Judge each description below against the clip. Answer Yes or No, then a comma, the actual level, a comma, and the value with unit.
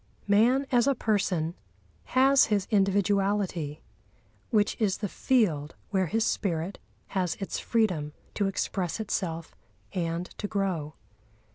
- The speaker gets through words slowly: Yes, slow, 120 wpm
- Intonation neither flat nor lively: Yes, average, 4.0 semitones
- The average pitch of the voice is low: No, high, 195 Hz